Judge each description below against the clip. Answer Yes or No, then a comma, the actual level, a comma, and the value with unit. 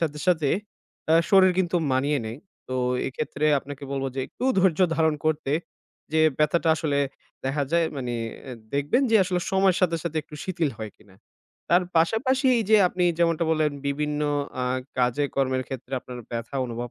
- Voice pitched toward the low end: No, medium, 150 Hz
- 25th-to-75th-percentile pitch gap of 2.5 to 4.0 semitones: No, average, 4.4 semitones